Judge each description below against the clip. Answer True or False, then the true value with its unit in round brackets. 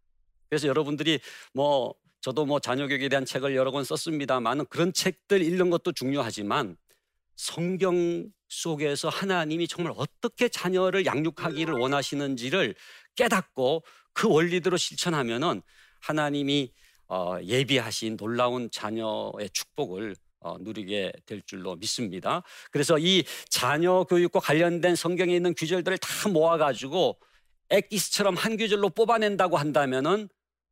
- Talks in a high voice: False (155 Hz)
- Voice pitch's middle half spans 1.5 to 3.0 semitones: False (5.4 semitones)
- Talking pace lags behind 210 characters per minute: False (310 characters per minute)